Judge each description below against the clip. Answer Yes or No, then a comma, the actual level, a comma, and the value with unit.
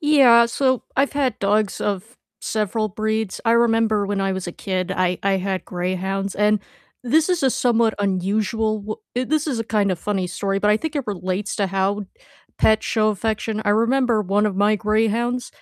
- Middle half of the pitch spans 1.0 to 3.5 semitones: Yes, average, 3.0 semitones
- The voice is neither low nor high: No, high, 215 Hz